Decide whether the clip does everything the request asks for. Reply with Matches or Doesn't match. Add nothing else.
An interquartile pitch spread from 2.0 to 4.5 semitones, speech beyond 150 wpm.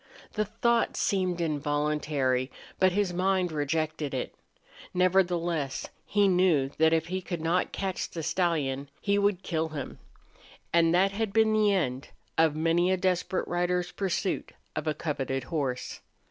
Doesn't match